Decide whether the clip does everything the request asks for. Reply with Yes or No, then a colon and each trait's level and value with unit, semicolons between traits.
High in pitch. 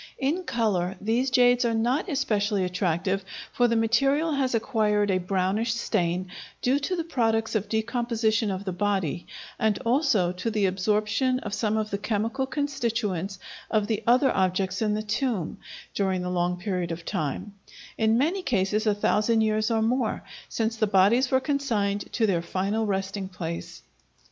Yes: high, 215 Hz